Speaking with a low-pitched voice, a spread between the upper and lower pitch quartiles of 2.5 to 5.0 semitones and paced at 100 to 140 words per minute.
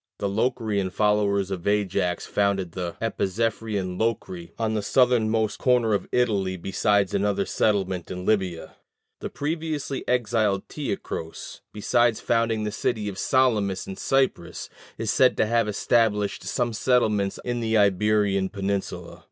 Yes: low, 105 Hz; average, 2.9 semitones; slow, 135 wpm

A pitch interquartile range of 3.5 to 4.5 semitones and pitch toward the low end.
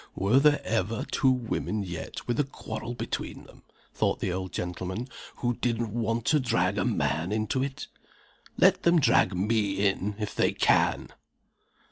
Yes: average, 4.0 semitones; low, 110 Hz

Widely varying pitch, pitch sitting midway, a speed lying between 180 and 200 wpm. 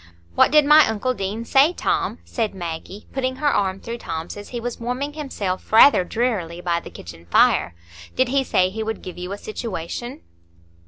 No: wide, 5.9 semitones; high, 220 Hz; average, 190 wpm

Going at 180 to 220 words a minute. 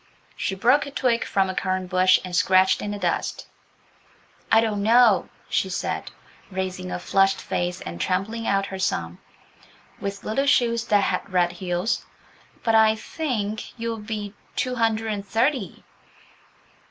No: average, 155 wpm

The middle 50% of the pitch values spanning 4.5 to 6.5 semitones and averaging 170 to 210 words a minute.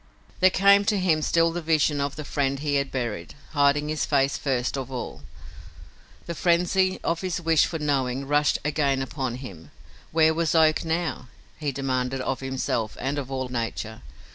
No: average, 3.5 semitones; average, 175 wpm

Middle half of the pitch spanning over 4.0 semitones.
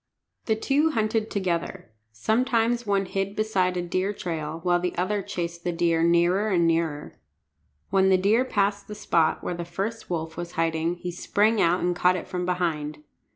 No: average, 3.2 semitones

